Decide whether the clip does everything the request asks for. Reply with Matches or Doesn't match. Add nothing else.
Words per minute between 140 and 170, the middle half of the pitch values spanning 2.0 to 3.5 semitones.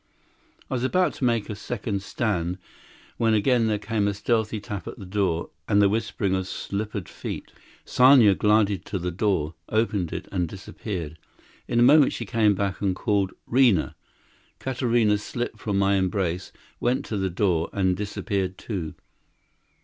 Matches